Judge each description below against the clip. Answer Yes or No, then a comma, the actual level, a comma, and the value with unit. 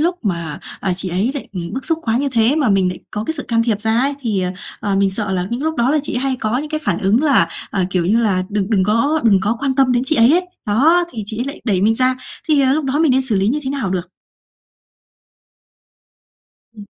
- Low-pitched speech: No, high, 230 Hz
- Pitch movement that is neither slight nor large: No, wide, 5.8 semitones